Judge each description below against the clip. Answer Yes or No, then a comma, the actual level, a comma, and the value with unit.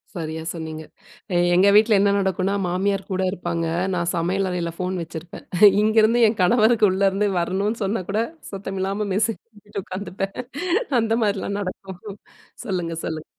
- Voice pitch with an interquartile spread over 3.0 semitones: No, average, 2.7 semitones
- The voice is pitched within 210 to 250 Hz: No, high, 195 Hz